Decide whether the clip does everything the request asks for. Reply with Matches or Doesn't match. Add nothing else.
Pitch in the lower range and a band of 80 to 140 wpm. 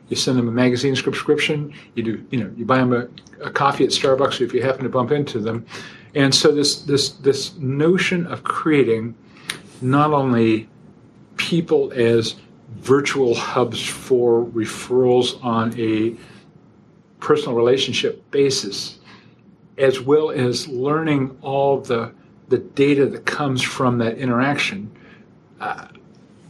Matches